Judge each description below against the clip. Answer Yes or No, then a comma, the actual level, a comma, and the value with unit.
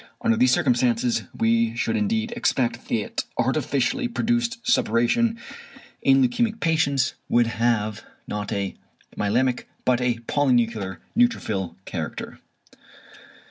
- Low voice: Yes, low, 125 Hz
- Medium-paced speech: No, slow, 105 wpm